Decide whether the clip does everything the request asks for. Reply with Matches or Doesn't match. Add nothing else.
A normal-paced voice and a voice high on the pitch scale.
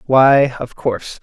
Doesn't match